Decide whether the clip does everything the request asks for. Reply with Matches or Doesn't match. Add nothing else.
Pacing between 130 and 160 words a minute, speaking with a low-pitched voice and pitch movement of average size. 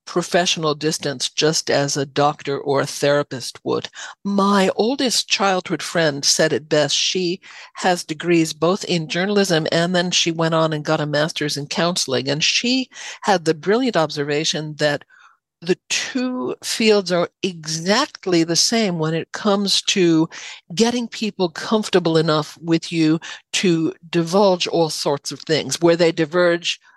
Doesn't match